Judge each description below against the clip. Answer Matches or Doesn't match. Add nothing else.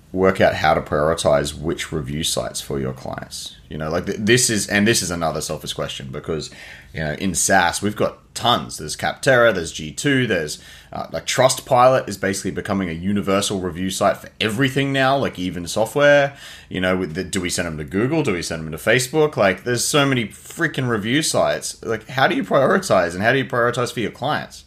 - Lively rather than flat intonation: Matches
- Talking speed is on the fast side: Matches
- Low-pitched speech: Matches